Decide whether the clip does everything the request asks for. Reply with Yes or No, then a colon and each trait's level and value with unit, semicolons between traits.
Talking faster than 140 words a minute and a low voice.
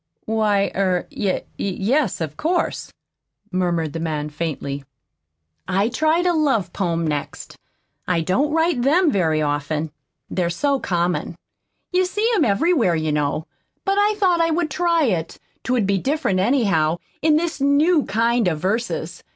No: average, 150 wpm; high, 205 Hz